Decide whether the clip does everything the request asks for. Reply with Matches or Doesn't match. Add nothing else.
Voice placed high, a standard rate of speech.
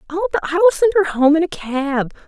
Doesn't match